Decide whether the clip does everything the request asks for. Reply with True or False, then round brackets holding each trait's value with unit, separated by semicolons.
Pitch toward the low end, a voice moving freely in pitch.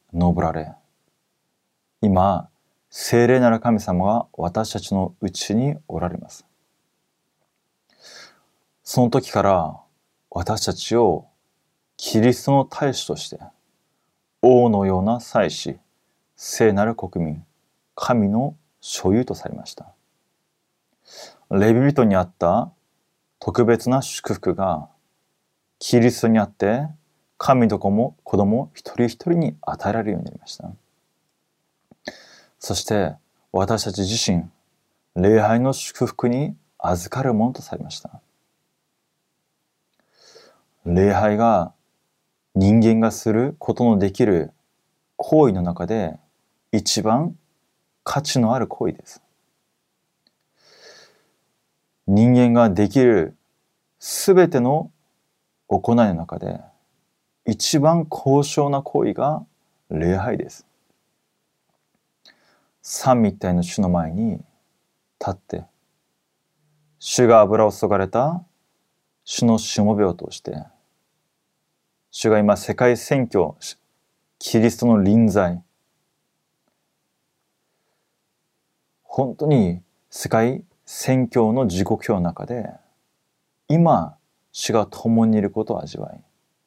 False (115 Hz; 4.5 semitones)